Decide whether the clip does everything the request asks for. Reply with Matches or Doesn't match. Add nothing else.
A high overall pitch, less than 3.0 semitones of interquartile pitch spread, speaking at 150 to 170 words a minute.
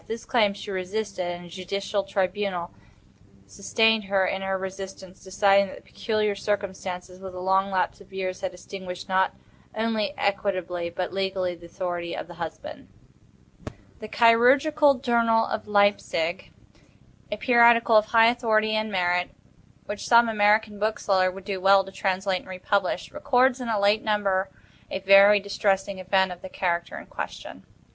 Matches